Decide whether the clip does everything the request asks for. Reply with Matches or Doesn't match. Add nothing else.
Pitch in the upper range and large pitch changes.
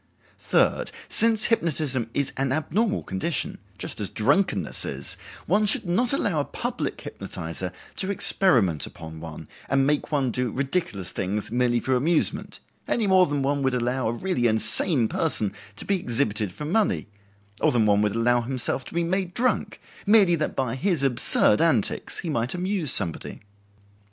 Doesn't match